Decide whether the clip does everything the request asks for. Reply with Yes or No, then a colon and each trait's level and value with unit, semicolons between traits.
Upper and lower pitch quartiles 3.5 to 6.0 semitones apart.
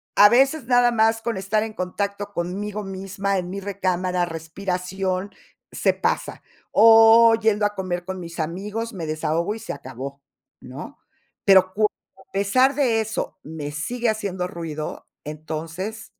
Yes: average, 3.9 semitones